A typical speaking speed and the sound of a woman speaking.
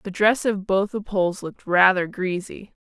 Yes: average, 190 wpm; female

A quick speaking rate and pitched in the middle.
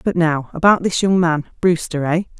No: average, 150 wpm; medium, 170 Hz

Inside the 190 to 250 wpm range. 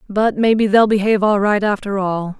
Yes: average, 200 wpm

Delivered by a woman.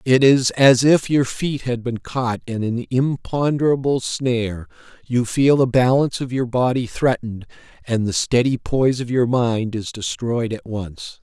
No: male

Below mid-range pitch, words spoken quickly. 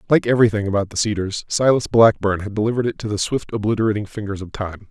Yes: low, 105 Hz; fast, 210 wpm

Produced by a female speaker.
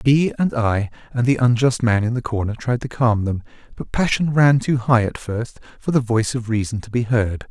No: male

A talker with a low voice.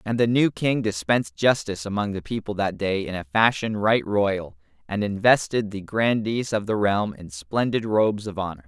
Yes: low, 105 Hz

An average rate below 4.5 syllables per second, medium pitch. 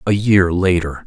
No: 4.2 syllables/s; very low, 90 Hz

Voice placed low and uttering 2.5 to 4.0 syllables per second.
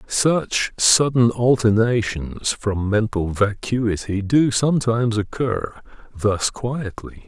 Yes: low, 115 Hz; 3.4 syllables/s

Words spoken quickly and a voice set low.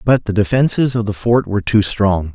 Yes: fast, 230 wpm; low, 105 Hz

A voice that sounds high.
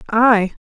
Yes: high, 220 Hz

